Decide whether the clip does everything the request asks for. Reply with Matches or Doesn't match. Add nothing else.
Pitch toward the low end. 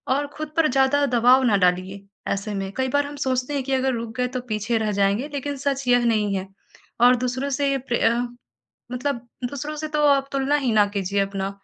Doesn't match